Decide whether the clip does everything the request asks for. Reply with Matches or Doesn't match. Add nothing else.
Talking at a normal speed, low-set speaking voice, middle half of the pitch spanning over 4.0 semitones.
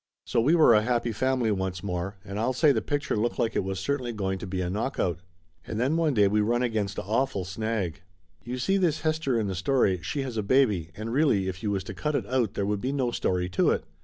Doesn't match